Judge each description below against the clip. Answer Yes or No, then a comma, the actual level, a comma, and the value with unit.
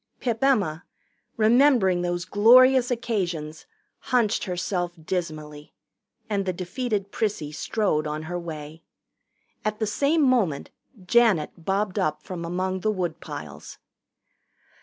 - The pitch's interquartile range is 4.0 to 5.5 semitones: Yes, average, 5.0 semitones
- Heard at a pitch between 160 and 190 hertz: Yes, medium, 185 Hz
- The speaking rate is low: Yes, slow, 115 wpm